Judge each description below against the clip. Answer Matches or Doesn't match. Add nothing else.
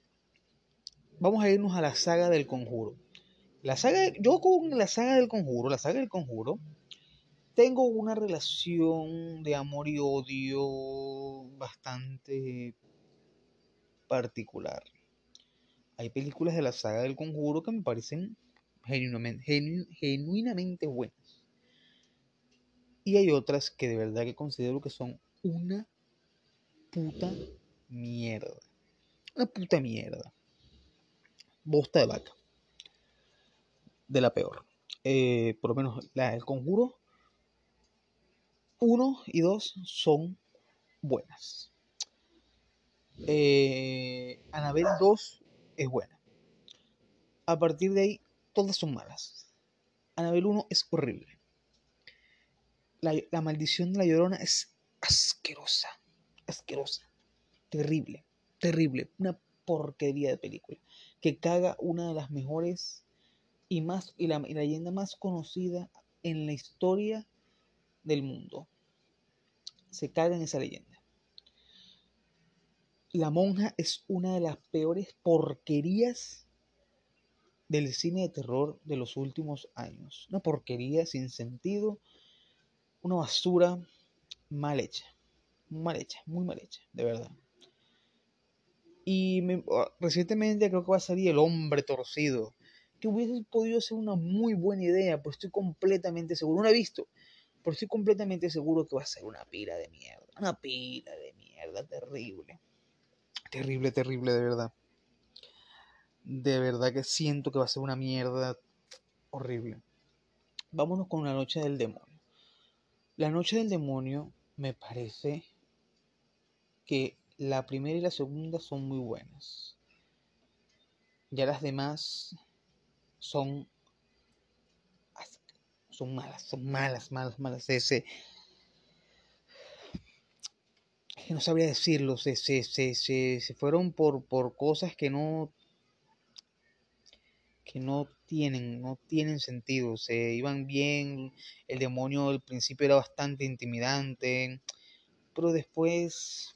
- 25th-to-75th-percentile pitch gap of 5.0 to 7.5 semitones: Matches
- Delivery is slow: Matches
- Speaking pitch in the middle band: Matches